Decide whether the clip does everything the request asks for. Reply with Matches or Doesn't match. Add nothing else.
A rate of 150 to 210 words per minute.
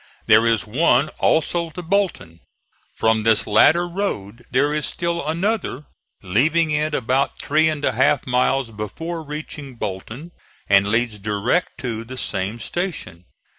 Doesn't match